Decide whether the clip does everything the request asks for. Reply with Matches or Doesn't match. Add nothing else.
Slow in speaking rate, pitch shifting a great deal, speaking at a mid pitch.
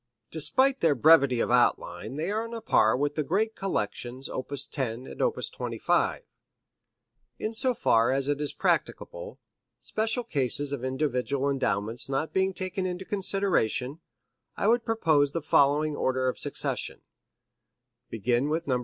Doesn't match